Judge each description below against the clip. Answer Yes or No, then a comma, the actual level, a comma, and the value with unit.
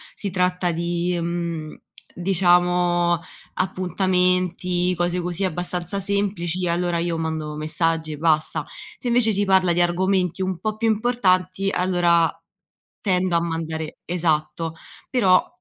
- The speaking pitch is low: No, medium, 175 Hz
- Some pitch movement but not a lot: No, narrow, 1.7 semitones